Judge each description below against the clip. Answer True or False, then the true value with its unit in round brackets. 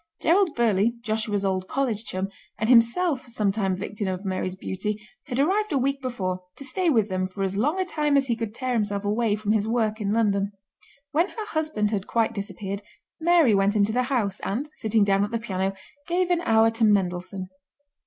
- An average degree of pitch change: True (4.8 semitones)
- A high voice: True (220 Hz)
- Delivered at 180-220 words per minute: True (205 wpm)